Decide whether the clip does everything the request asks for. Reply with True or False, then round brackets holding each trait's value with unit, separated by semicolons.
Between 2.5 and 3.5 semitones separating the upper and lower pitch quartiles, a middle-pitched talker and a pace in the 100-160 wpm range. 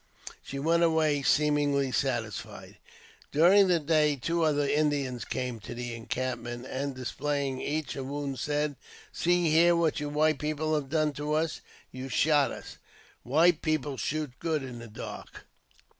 True (2.8 semitones; 145 Hz; 155 wpm)